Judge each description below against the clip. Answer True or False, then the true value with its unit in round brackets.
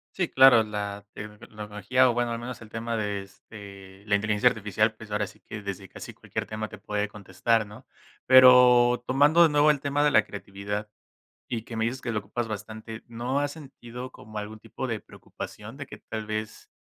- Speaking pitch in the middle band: False (110 Hz)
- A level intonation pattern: False (3.1 semitones)